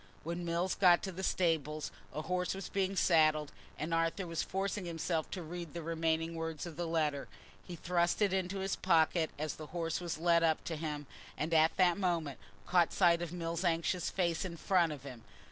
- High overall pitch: No, medium, 170 Hz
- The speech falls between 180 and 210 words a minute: Yes, average, 200 wpm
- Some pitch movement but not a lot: No, narrow, 2.0 semitones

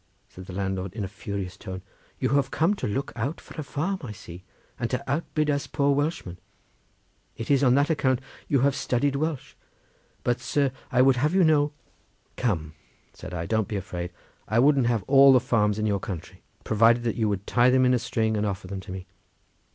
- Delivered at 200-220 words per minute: Yes, fast, 205 wpm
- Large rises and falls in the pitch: Yes, wide, 5.8 semitones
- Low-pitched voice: Yes, low, 120 Hz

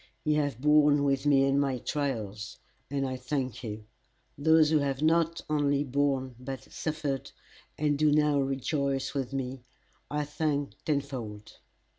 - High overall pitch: No, medium, 140 Hz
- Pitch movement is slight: Yes, narrow, 2.0 semitones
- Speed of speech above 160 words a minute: No, average, 145 wpm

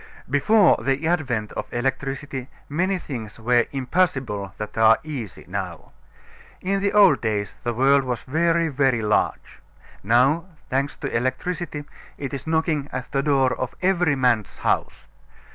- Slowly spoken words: No, average, 145 wpm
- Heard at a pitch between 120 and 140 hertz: Yes, low, 135 Hz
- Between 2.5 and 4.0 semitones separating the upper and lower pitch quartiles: No, average, 4.8 semitones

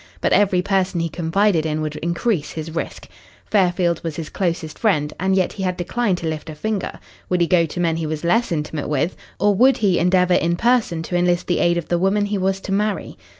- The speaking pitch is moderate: Yes, medium, 175 Hz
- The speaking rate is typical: No, fast, 230 wpm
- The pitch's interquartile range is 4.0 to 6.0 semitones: No, average, 2.9 semitones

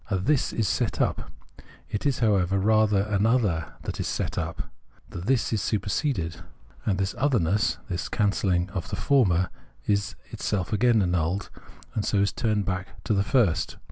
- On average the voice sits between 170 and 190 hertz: No, low, 100 Hz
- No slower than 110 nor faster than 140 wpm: No, average, 165 wpm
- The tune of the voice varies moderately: Yes, average, 3.2 semitones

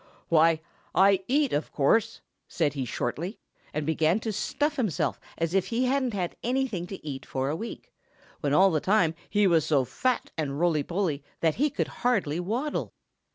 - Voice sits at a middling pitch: Yes, medium, 180 Hz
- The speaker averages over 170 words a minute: Yes, average, 180 wpm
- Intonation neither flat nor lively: No, wide, 6.6 semitones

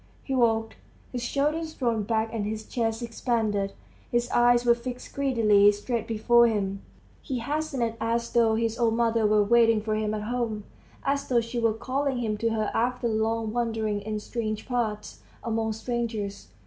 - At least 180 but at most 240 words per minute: No, average, 170 wpm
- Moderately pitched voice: No, high, 230 Hz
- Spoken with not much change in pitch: Yes, narrow, 1.8 semitones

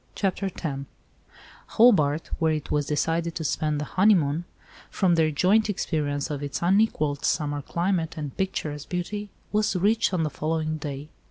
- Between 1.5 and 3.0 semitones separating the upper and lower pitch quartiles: No, average, 4.2 semitones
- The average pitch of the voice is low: No, medium, 160 Hz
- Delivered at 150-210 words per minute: Yes, average, 155 wpm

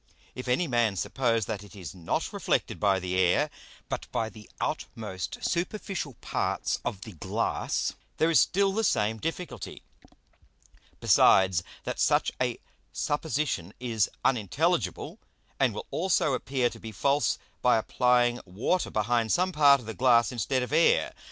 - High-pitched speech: No, low, 120 Hz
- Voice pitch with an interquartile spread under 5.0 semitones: No, wide, 5.6 semitones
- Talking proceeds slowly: No, average, 150 wpm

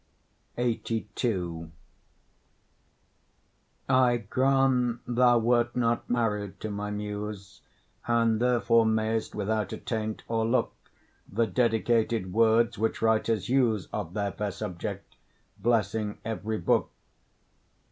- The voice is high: No, low, 110 Hz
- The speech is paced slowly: Yes, slow, 95 wpm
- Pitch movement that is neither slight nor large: No, narrow, 2.2 semitones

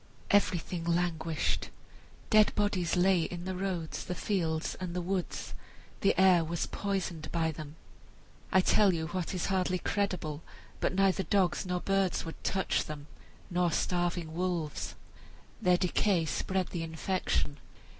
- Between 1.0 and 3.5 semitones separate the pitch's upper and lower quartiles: Yes, narrow, 2.4 semitones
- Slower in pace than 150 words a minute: Yes, average, 140 wpm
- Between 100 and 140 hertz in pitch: No, medium, 180 Hz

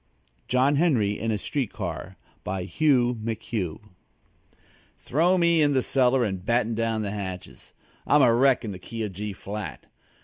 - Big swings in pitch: No, average, 4.6 semitones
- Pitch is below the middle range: Yes, low, 115 Hz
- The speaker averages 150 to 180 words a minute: Yes, average, 165 wpm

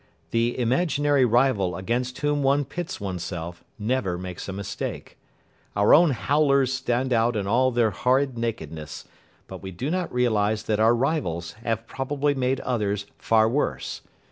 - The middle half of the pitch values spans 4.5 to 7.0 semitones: Yes, average, 4.8 semitones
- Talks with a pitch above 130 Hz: No, low, 120 Hz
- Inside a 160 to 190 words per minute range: No, average, 150 wpm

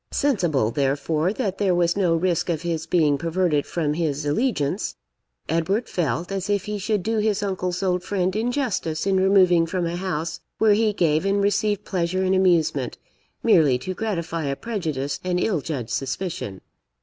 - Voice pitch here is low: No, medium, 180 Hz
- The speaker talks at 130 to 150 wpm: No, average, 170 wpm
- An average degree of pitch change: Yes, average, 3.8 semitones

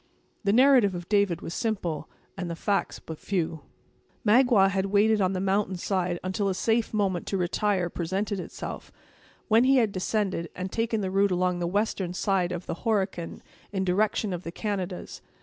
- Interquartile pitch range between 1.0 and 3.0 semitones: Yes, average, 2.7 semitones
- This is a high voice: Yes, high, 195 Hz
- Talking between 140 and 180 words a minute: Yes, average, 175 wpm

